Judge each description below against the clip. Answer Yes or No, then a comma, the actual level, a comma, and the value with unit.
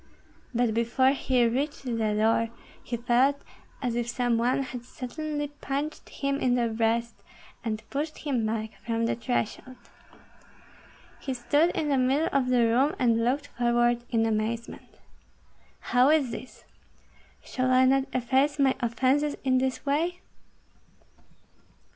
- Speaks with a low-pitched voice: No, very high, 250 Hz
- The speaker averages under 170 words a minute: Yes, average, 140 wpm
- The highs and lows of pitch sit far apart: No, average, 2.9 semitones